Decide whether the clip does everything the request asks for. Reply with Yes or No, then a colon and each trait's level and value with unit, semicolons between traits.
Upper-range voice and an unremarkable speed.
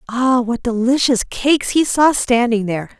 Yes: high, 245 Hz; average, 160 wpm